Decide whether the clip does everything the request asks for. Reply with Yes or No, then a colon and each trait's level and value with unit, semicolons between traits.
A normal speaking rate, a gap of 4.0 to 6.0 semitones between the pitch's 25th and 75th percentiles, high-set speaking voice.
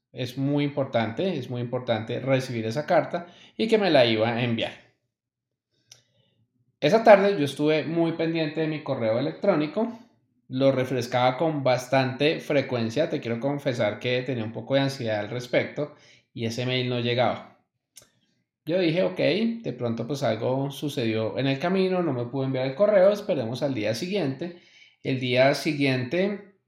No: average, 160 wpm; average, 4.3 semitones; low, 135 Hz